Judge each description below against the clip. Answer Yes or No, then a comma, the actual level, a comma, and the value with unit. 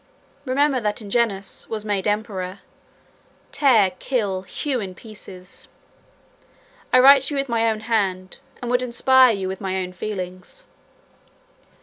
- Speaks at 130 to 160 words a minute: Yes, average, 140 wpm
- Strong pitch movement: No, average, 4.8 semitones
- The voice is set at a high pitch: Yes, high, 215 Hz